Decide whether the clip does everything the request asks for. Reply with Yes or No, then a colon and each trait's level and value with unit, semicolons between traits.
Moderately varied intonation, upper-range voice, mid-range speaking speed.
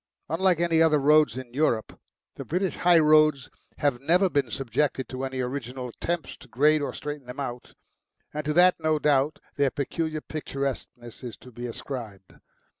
No: average, 3.5 semitones; medium, 140 Hz; average, 170 wpm